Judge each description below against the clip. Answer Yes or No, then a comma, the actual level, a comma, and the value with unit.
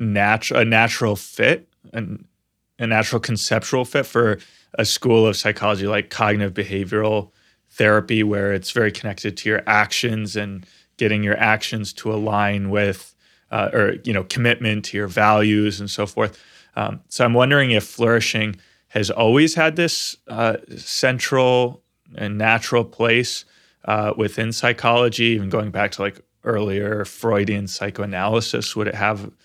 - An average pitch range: No, narrow, 2.1 semitones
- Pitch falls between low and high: No, low, 105 Hz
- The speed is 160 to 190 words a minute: No, average, 145 wpm